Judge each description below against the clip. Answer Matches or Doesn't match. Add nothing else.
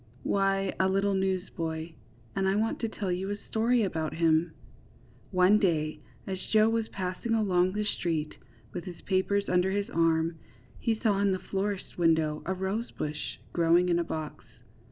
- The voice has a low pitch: Doesn't match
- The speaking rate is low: Doesn't match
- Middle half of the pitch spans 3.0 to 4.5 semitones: Matches